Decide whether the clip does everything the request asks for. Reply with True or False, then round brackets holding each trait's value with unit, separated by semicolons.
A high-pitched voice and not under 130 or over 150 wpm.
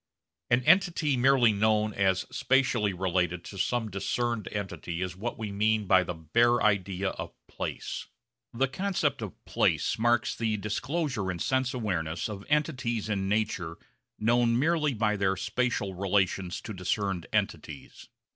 False (105 Hz; 145 wpm)